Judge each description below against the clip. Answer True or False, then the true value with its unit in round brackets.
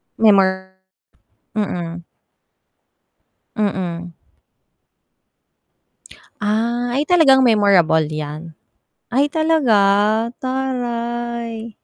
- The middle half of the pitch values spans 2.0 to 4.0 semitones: False (4.4 semitones)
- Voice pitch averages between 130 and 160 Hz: False (220 Hz)